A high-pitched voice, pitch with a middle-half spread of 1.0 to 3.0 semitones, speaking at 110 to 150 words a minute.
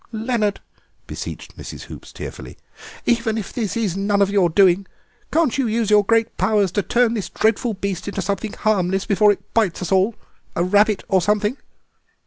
No: high, 205 Hz; narrow, 2.5 semitones; average, 170 wpm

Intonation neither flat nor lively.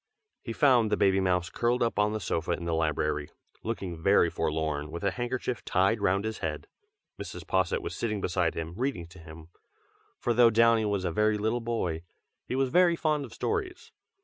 No: wide, 5.9 semitones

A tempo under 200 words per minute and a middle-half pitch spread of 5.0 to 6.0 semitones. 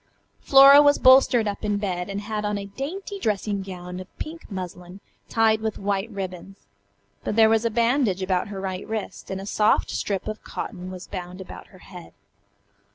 No: average, 185 wpm; average, 3.1 semitones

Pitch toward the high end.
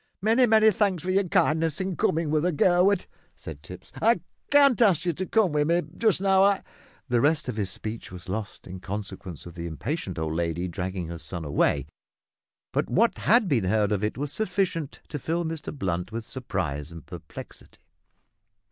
No: medium, 145 Hz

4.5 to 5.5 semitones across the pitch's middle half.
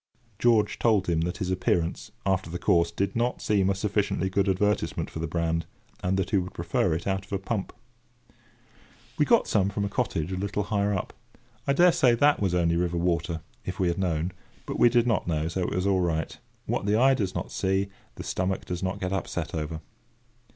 No: average, 2.8 semitones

